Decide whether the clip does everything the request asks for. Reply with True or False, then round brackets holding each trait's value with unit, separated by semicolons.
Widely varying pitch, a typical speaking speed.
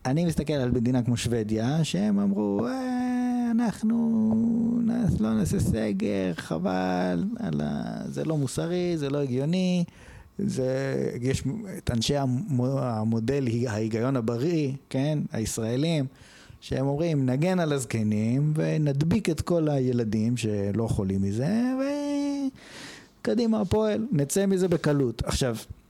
True (8.3 semitones; 110 wpm)